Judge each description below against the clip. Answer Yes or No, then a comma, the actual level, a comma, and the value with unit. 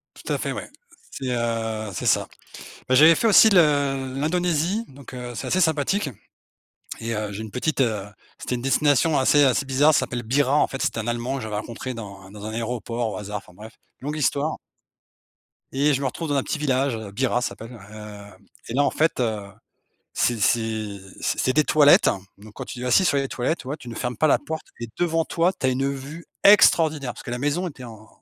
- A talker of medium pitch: No, low, 130 Hz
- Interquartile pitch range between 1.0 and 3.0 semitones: No, average, 4.6 semitones